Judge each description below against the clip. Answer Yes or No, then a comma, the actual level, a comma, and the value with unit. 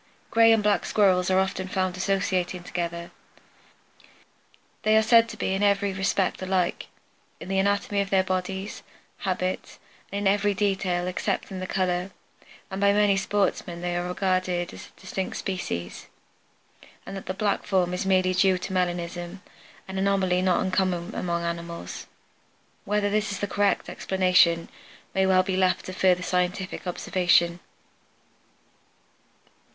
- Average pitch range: No, narrow, 1.6 semitones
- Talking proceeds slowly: No, average, 145 wpm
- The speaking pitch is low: No, medium, 185 Hz